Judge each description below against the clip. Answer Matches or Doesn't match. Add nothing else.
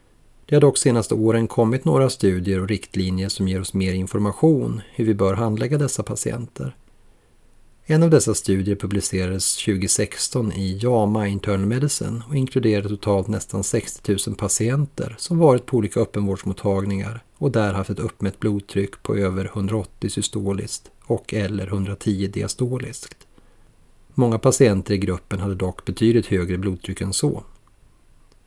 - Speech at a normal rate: Matches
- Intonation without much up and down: Doesn't match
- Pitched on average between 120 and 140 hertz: Doesn't match